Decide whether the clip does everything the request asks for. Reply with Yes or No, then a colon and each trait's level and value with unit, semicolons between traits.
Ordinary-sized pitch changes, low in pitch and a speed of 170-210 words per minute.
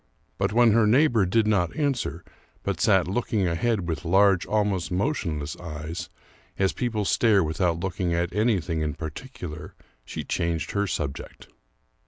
No: average, 4.6 semitones; very low, 95 Hz; average, 145 wpm